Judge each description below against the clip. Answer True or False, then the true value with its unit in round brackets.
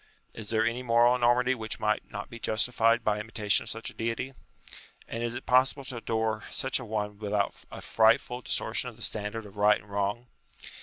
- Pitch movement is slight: True (2.3 semitones)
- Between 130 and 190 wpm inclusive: False (200 wpm)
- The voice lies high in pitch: False (115 Hz)